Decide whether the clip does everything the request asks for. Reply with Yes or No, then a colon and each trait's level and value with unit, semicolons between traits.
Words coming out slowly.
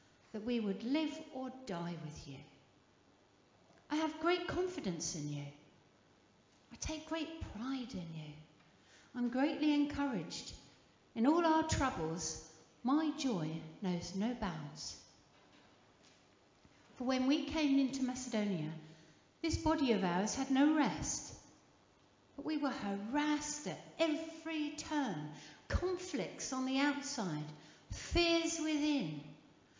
Yes: slow, 115 wpm